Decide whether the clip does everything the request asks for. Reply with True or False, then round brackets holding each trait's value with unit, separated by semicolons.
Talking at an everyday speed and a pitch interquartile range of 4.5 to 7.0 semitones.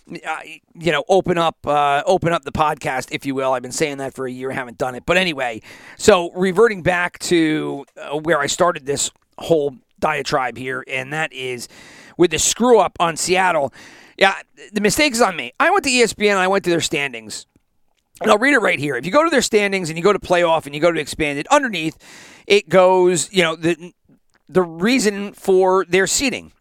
False (215 wpm; 5.1 semitones)